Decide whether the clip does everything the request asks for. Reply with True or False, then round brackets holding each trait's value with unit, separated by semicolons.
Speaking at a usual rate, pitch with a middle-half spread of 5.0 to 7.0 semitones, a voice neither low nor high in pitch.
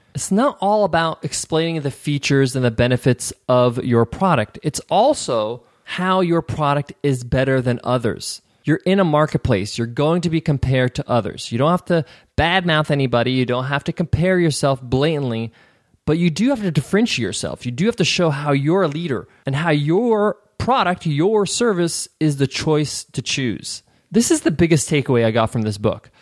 True (190 wpm; 5.3 semitones; 150 Hz)